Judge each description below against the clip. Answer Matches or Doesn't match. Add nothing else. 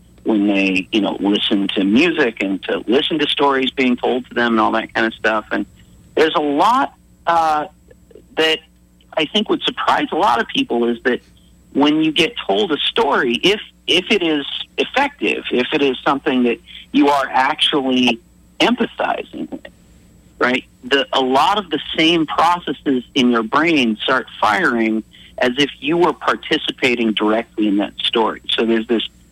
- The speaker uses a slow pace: Doesn't match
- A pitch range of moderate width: Doesn't match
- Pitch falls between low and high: Doesn't match